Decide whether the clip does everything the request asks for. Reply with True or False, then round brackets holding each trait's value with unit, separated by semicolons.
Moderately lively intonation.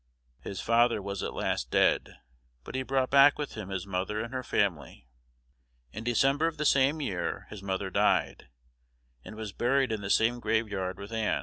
True (5.0 semitones)